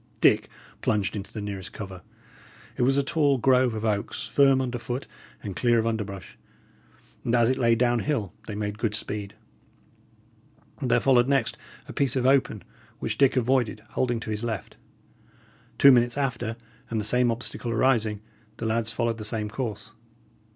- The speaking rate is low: No, average, 170 wpm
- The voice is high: No, low, 115 Hz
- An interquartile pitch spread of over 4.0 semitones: No, average, 3.1 semitones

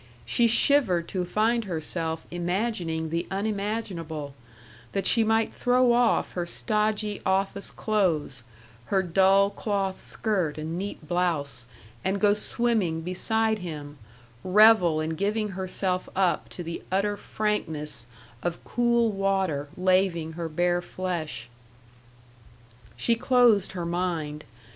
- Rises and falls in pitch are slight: No, average, 4.2 semitones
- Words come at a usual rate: No, slow, 120 wpm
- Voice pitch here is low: No, medium, 185 Hz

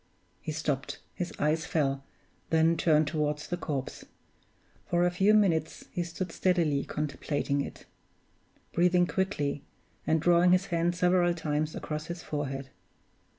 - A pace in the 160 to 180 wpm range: No, slow, 135 wpm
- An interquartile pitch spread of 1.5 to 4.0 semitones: Yes, average, 2.9 semitones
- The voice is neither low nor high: Yes, medium, 160 Hz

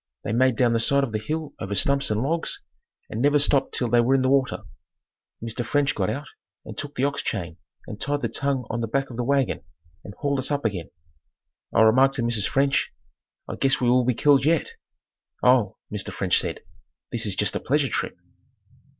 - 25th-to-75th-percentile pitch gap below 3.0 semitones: No, average, 3.4 semitones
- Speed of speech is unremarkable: No, fast, 210 wpm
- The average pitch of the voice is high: No, low, 130 Hz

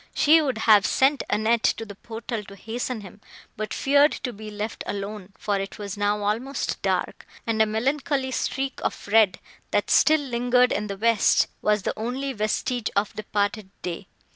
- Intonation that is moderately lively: Yes, average, 3.5 semitones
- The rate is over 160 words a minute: Yes, average, 175 wpm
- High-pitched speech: Yes, high, 220 Hz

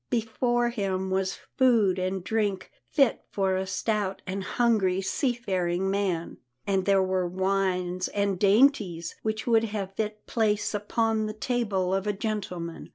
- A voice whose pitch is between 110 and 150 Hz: No, high, 195 Hz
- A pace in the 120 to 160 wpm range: Yes, average, 155 wpm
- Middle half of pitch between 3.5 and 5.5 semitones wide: No, average, 2.8 semitones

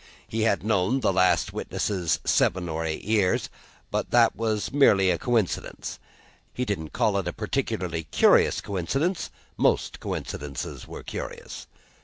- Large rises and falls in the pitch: No, average, 4.2 semitones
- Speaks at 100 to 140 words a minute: Yes, slow, 135 wpm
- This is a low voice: Yes, low, 100 Hz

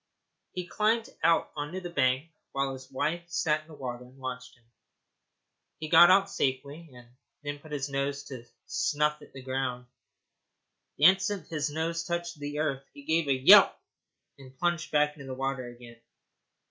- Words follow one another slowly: No, average, 175 wpm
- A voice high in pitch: No, medium, 145 Hz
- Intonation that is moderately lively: Yes, average, 4.0 semitones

